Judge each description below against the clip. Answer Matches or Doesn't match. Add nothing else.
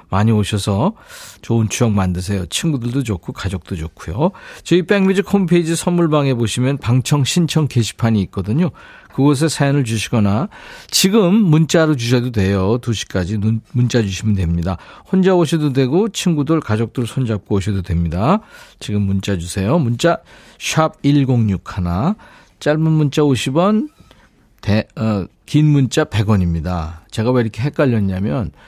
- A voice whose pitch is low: Matches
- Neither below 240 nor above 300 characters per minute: Matches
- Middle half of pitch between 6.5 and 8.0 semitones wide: Matches